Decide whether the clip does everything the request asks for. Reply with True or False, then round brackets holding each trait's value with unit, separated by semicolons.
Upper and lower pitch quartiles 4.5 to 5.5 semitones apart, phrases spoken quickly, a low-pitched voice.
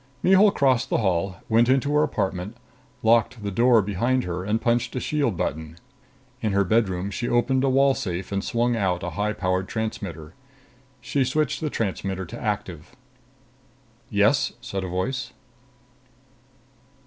False (5.1 semitones; 150 wpm; 110 Hz)